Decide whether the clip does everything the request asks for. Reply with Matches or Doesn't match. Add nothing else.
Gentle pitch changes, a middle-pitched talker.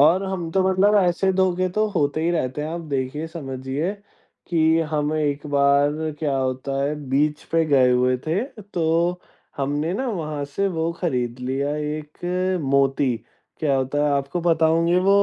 Doesn't match